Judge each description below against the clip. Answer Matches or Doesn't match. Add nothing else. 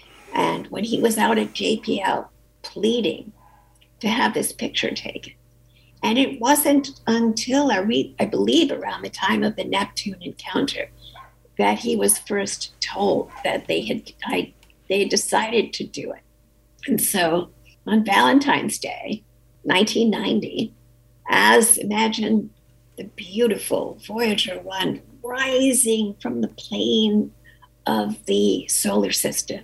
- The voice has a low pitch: Doesn't match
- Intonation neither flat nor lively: Doesn't match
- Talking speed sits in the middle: Doesn't match